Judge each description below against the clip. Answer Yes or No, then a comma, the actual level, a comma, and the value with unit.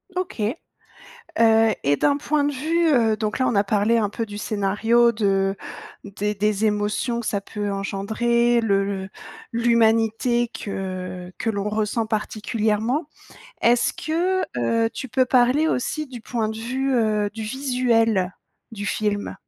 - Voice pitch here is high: Yes, high, 225 Hz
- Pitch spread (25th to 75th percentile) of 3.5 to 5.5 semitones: No, average, 2.8 semitones